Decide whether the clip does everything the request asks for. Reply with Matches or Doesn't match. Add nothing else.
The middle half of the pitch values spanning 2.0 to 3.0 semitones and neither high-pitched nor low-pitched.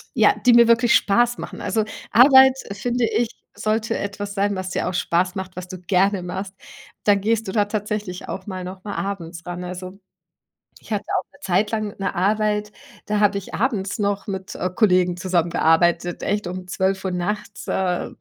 Doesn't match